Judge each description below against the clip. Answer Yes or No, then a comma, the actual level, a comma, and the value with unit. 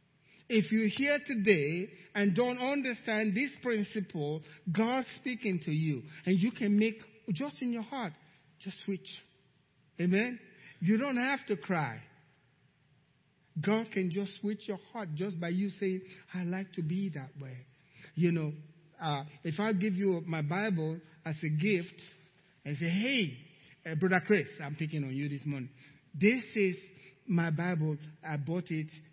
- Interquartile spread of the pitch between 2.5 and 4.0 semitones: No, average, 5.2 semitones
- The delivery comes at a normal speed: Yes, average, 155 wpm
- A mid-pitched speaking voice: Yes, medium, 180 Hz